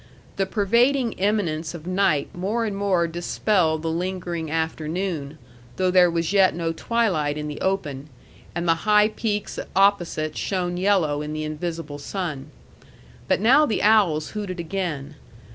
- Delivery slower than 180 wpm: Yes, average, 145 wpm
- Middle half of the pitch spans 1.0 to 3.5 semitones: No, average, 4.2 semitones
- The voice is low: No, medium, 175 Hz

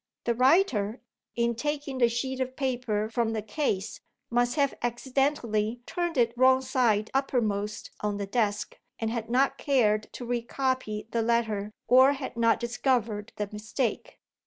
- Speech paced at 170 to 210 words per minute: No, average, 155 wpm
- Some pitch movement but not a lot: Yes, average, 3.3 semitones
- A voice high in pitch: Yes, high, 235 Hz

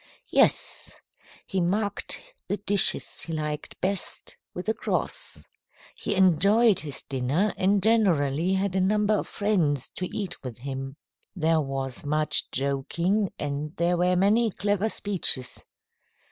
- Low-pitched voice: No, medium, 180 Hz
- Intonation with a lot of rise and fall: Yes, wide, 5.8 semitones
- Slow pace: Yes, slow, 130 wpm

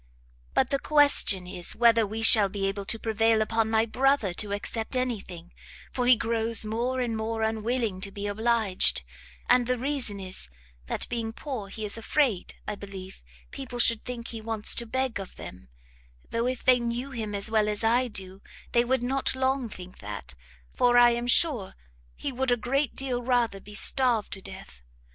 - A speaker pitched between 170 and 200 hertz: No, high, 225 Hz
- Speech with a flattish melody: No, average, 3.3 semitones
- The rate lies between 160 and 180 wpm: No, average, 190 wpm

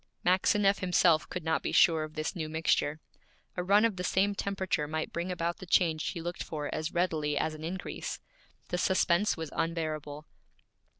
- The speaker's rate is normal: Yes, average, 180 wpm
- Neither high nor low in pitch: Yes, medium, 170 Hz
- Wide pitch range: No, average, 2.9 semitones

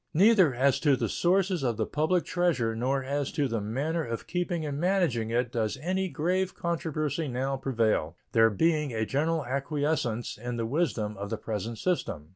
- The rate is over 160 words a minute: Yes, average, 180 wpm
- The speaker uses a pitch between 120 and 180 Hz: Yes, medium, 140 Hz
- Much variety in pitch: Yes, wide, 6.2 semitones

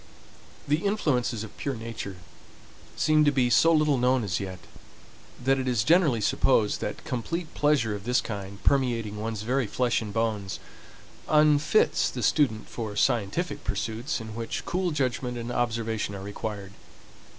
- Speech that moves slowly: No, average, 150 wpm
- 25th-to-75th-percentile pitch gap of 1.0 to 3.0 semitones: No, average, 4.6 semitones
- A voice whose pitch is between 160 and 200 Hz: No, low, 120 Hz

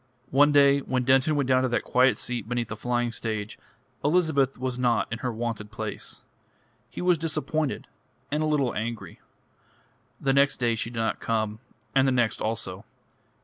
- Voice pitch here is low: Yes, low, 125 Hz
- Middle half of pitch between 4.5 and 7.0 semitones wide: No, average, 3.5 semitones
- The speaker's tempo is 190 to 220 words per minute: No, average, 175 wpm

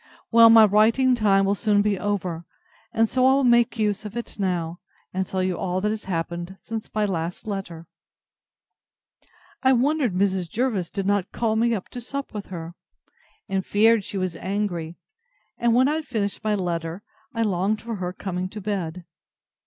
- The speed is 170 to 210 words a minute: Yes, average, 180 wpm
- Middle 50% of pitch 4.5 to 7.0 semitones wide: No, average, 3.6 semitones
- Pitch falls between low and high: No, high, 205 Hz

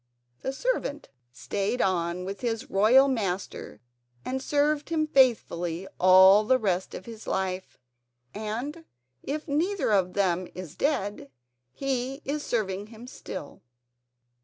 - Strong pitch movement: Yes, wide, 6.4 semitones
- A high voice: Yes, high, 220 Hz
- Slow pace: Yes, slow, 125 wpm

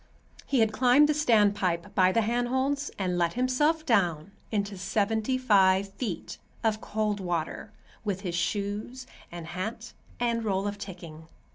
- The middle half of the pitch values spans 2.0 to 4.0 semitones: No, average, 4.5 semitones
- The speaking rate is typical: Yes, average, 145 wpm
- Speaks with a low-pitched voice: No, high, 205 Hz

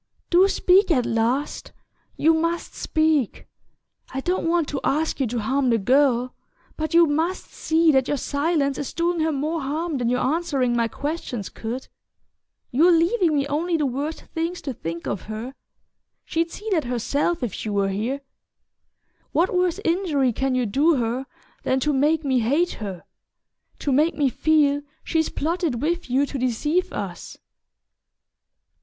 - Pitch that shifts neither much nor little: Yes, average, 4.6 semitones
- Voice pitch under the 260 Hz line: No, very high, 290 Hz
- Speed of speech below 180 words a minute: Yes, average, 160 wpm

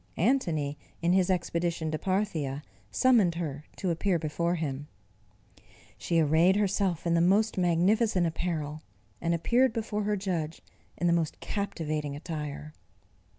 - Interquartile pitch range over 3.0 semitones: Yes, average, 3.8 semitones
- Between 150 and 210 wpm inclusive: No, slow, 135 wpm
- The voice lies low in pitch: No, medium, 170 Hz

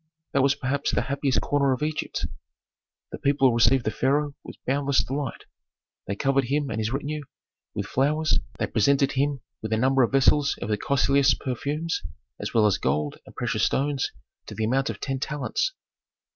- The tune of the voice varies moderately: No, narrow, 2.2 semitones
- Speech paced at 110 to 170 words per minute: No, average, 180 wpm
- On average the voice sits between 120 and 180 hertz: Yes, low, 135 Hz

